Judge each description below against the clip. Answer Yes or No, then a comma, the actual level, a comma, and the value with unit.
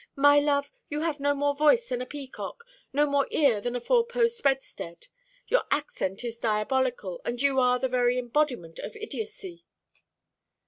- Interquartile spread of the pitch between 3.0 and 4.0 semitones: Yes, average, 3.5 semitones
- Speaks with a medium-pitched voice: No, very high, 280 Hz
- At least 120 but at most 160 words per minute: No, average, 170 wpm